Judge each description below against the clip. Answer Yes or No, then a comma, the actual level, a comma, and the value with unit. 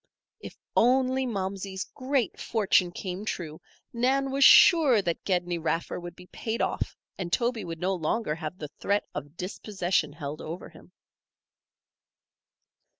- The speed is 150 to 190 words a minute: No, average, 140 wpm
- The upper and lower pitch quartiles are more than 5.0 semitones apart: Yes, wide, 5.5 semitones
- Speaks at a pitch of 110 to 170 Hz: No, high, 190 Hz